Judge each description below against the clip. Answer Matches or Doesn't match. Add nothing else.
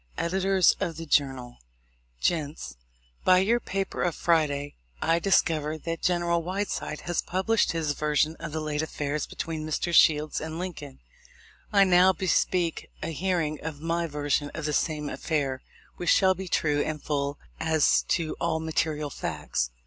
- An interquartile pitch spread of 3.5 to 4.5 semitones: Doesn't match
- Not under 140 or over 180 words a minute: Matches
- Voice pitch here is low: Doesn't match